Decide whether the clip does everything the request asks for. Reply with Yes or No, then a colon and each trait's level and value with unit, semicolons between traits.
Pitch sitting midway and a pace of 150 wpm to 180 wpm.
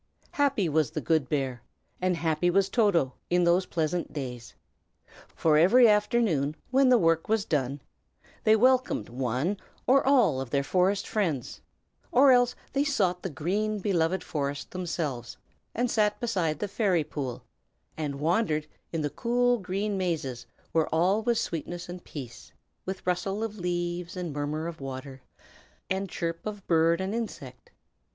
Yes: medium, 175 Hz; average, 155 wpm